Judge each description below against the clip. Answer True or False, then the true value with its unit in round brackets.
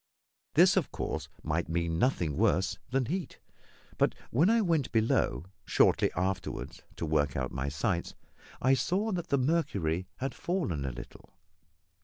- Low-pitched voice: True (95 Hz)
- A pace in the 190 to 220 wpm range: False (150 wpm)